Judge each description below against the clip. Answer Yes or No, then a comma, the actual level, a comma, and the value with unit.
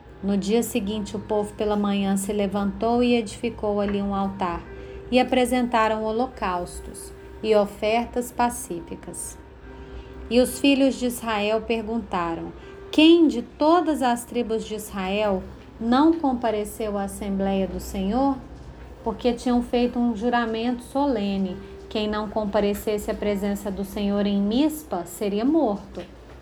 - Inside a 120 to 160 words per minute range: Yes, average, 125 wpm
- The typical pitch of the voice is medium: No, high, 220 Hz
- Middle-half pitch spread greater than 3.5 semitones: No, average, 3.2 semitones